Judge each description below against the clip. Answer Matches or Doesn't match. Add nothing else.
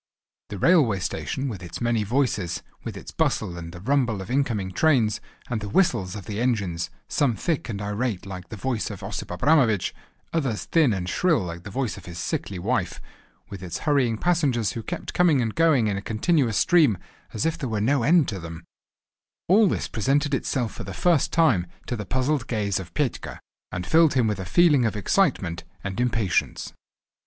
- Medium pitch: Doesn't match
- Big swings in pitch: Matches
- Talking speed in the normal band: Matches